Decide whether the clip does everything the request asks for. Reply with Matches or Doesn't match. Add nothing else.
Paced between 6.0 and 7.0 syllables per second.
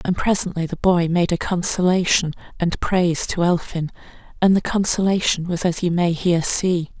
Doesn't match